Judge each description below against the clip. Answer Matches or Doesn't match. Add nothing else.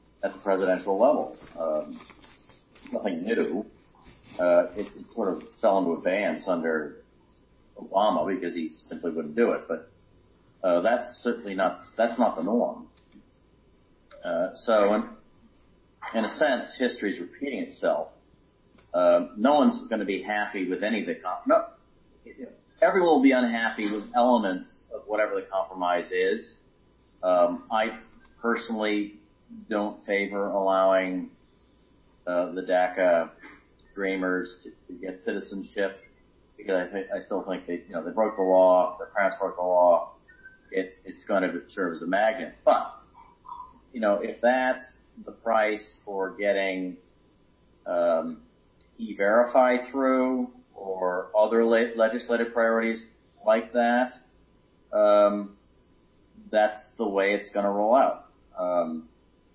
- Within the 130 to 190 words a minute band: Matches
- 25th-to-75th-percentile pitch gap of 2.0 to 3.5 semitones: Doesn't match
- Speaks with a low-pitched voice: Matches